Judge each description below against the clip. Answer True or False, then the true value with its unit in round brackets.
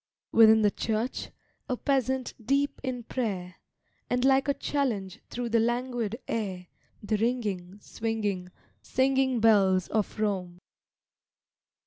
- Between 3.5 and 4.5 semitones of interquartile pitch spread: True (3.9 semitones)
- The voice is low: False (225 Hz)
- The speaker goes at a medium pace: False (115 wpm)